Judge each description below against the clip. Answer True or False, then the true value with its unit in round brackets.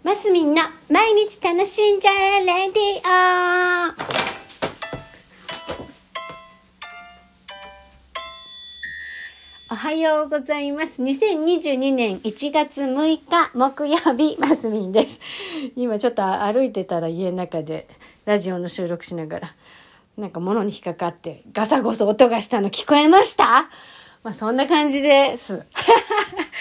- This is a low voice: False (270 Hz)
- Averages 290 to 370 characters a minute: False (235 characters per minute)